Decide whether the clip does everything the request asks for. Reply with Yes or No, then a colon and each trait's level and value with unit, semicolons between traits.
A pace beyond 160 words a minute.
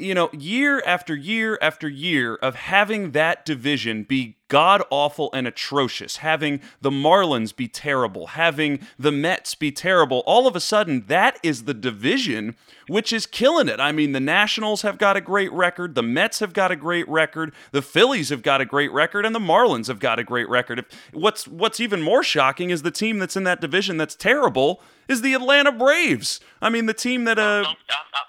Yes: average, 195 wpm